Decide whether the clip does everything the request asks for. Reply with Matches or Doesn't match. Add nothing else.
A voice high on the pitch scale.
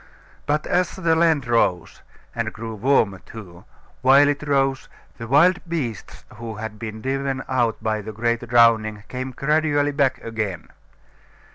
Doesn't match